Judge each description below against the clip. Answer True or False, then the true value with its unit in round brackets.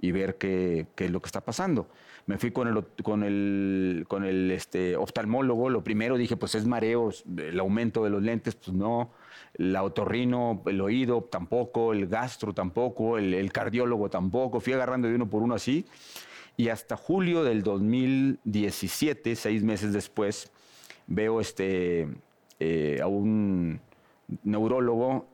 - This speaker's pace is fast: False (155 wpm)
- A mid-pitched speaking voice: False (110 Hz)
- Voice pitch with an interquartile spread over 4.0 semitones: False (3.5 semitones)